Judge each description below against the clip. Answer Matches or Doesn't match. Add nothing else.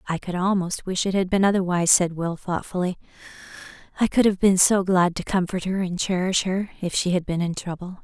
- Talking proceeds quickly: Matches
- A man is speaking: Doesn't match